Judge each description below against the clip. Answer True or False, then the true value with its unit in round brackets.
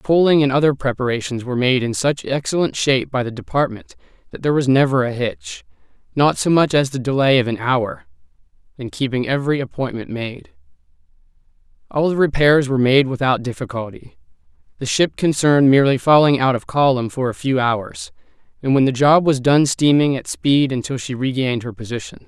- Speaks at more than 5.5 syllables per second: True (5.8 syllables/s)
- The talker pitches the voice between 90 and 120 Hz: False (135 Hz)